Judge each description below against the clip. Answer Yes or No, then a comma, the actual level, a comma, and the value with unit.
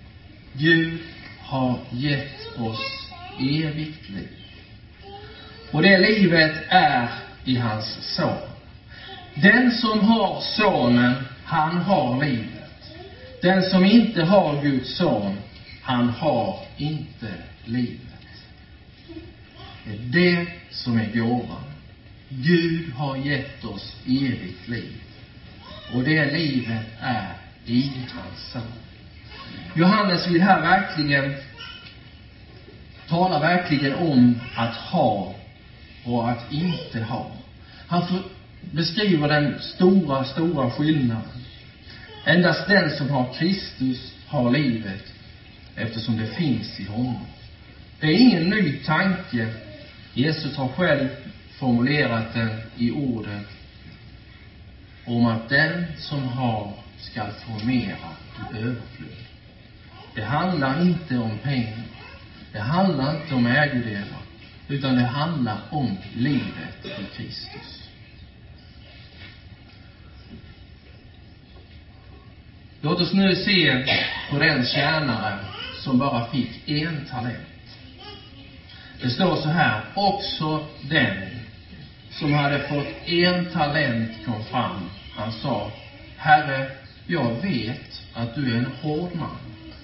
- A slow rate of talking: Yes, slow, 105 wpm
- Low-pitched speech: Yes, low, 125 Hz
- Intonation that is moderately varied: No, wide, 5.7 semitones